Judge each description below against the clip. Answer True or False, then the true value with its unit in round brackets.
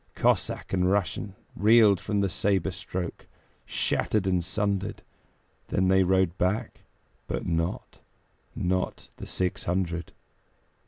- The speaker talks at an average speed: False (115 wpm)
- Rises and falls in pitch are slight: True (1.9 semitones)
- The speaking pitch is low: True (95 Hz)